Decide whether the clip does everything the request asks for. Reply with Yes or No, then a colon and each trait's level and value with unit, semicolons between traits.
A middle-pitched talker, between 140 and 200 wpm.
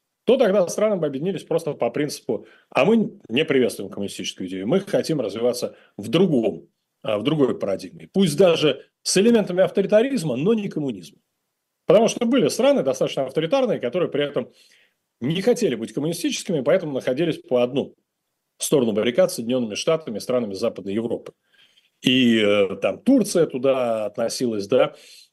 Yes: medium, 180 Hz; average, 145 wpm